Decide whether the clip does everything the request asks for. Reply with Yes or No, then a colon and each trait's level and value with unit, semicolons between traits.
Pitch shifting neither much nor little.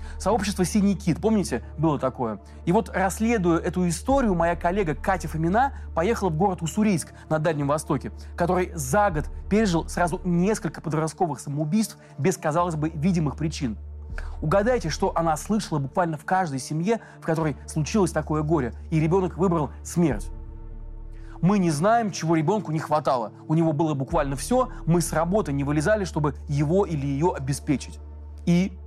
Yes: average, 5.0 semitones